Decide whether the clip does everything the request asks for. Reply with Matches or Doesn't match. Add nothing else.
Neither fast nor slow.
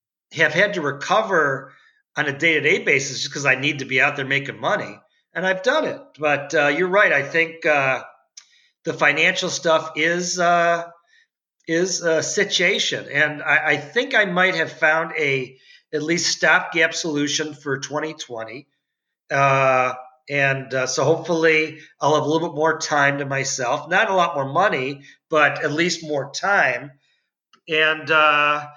Matches